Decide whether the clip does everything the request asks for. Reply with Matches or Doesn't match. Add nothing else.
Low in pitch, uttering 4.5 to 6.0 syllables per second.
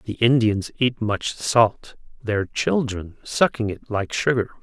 Doesn't match